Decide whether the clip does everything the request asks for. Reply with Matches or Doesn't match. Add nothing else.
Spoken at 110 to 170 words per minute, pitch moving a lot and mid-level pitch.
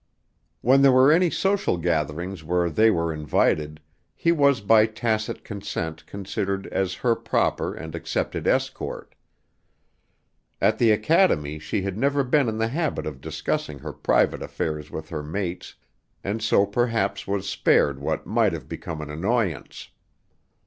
Doesn't match